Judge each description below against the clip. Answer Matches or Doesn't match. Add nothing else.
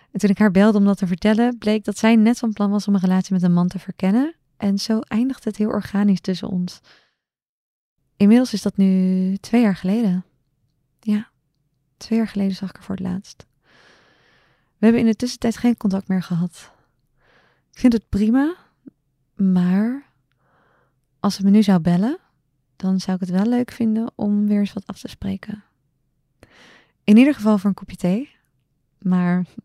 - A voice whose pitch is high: Matches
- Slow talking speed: Doesn't match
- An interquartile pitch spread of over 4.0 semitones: Doesn't match